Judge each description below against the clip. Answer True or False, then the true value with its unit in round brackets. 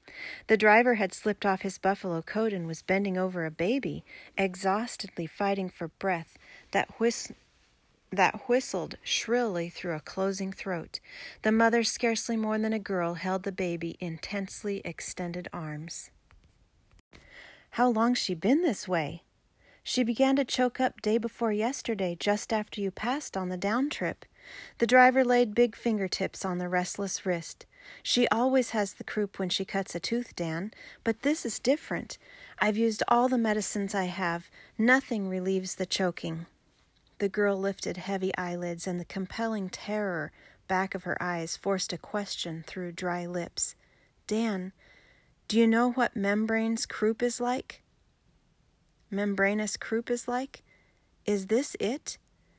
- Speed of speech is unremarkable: True (150 wpm)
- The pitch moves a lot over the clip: False (3.9 semitones)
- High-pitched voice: True (200 Hz)